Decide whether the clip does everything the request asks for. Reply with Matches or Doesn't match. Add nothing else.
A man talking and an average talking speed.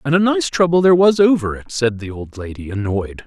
Doesn't match